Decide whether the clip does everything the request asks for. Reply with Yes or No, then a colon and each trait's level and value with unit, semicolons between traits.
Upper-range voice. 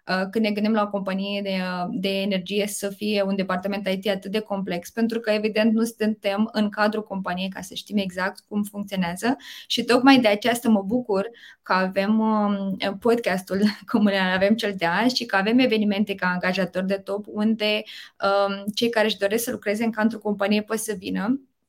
Yes: high, 205 Hz